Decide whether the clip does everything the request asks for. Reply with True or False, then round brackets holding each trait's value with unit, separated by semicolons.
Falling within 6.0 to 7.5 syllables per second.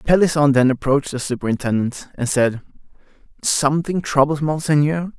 False (5.5 syllables/s)